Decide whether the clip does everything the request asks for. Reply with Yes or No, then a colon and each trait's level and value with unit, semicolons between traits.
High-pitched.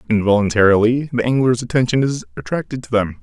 No: low, 115 Hz